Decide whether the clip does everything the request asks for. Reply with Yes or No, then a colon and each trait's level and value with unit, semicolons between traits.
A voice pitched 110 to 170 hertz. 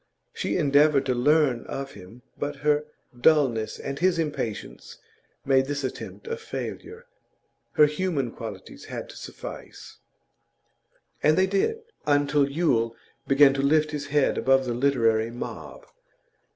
Yes: medium, 140 Hz